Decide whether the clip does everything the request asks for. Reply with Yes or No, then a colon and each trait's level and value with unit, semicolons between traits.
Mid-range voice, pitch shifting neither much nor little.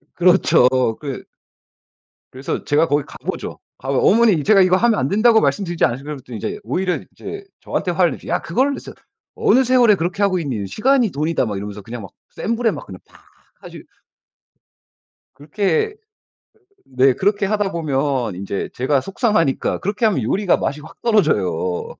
No: medium, 170 Hz; wide, 7.9 semitones